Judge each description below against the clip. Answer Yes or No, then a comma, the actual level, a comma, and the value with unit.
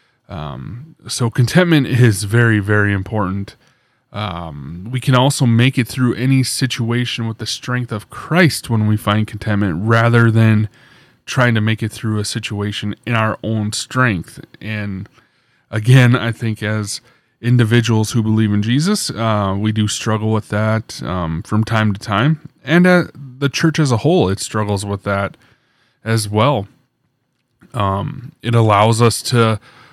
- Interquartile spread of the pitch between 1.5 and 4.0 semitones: Yes, average, 3.3 semitones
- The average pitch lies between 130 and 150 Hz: No, low, 115 Hz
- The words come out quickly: No, average, 155 wpm